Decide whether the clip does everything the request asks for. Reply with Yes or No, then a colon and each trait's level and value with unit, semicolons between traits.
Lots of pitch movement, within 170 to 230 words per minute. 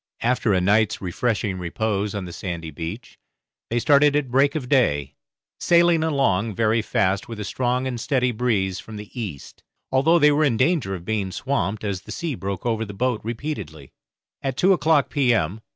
Yes: wide, 5.7 semitones; average, 185 wpm